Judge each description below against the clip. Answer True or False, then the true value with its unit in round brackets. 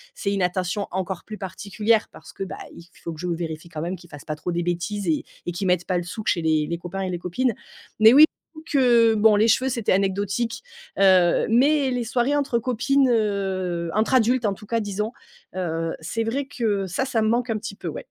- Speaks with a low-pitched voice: False (200 Hz)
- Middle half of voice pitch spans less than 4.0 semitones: False (4.7 semitones)